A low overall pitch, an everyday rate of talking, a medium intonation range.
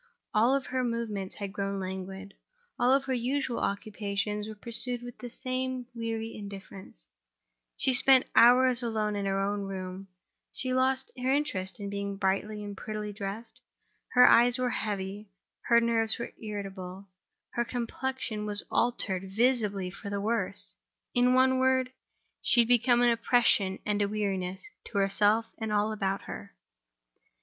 No: high, 215 Hz; average, 150 wpm; average, 3.6 semitones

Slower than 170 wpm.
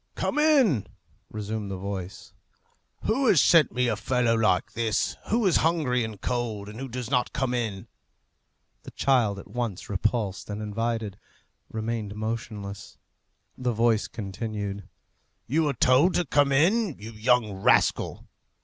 Yes: average, 145 wpm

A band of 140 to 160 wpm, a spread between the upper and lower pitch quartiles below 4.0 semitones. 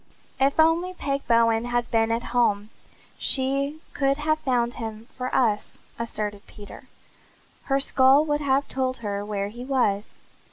Yes: average, 150 wpm; average, 3.6 semitones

